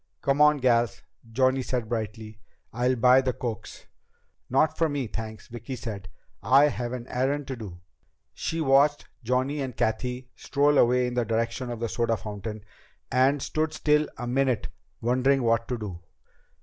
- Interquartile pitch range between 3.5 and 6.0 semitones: No, average, 2.9 semitones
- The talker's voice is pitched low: Yes, low, 125 Hz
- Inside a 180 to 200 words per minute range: No, average, 160 wpm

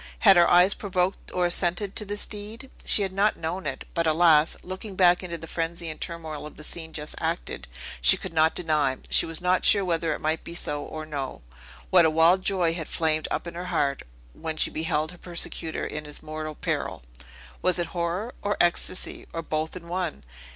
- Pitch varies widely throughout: No, average, 2.7 semitones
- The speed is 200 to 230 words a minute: Yes, fast, 205 wpm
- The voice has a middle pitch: Yes, medium, 170 Hz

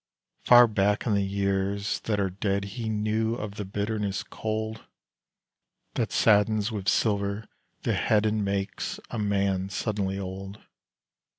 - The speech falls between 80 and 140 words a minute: Yes, slow, 135 wpm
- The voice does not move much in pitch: Yes, narrow, 1.7 semitones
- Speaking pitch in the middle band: No, low, 100 Hz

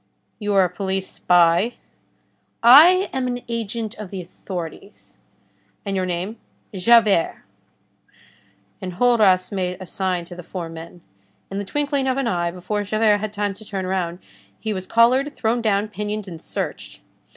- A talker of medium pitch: No, high, 200 Hz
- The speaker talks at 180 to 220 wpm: No, average, 155 wpm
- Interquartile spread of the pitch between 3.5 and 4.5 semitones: Yes, average, 3.9 semitones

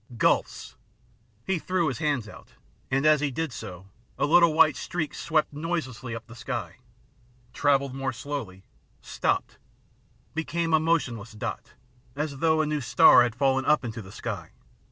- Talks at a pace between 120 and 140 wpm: No, average, 160 wpm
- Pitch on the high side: No, medium, 140 Hz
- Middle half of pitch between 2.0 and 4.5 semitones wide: No, average, 5.0 semitones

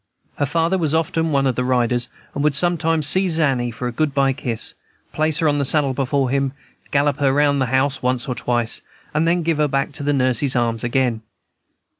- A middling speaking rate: No, fast, 215 wpm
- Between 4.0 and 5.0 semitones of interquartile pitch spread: No, average, 3.2 semitones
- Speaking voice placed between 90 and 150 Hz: Yes, medium, 140 Hz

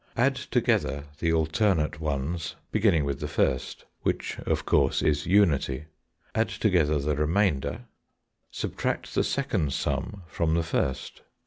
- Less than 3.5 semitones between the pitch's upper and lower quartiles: No, average, 4.5 semitones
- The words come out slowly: Yes, slow, 130 wpm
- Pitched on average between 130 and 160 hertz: No, very low, 80 Hz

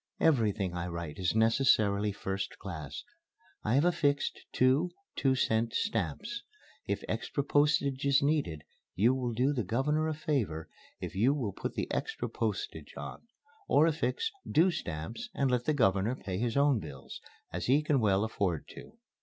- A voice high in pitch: No, low, 125 Hz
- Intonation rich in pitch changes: Yes, wide, 6.6 semitones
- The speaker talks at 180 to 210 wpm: No, average, 160 wpm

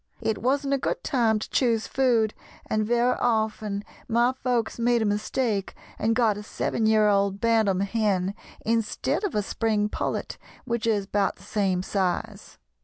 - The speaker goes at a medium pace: Yes, average, 165 wpm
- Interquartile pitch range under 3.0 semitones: Yes, narrow, 2.5 semitones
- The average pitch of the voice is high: Yes, high, 220 Hz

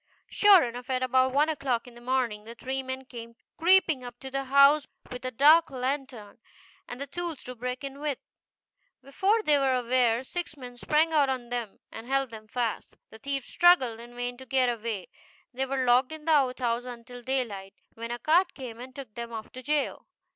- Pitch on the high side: Yes, very high, 255 Hz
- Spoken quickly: Yes, fast, 220 wpm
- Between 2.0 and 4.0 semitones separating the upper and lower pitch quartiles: Yes, narrow, 2.6 semitones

